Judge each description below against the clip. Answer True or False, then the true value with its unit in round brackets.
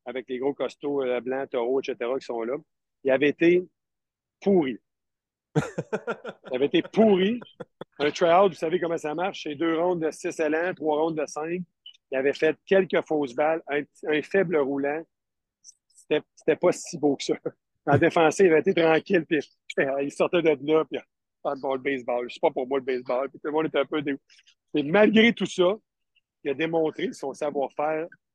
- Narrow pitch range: False (3.6 semitones)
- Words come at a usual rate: True (200 wpm)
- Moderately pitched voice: True (155 Hz)